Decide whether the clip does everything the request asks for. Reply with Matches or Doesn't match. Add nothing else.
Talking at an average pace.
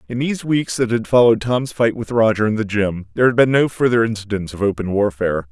Doesn't match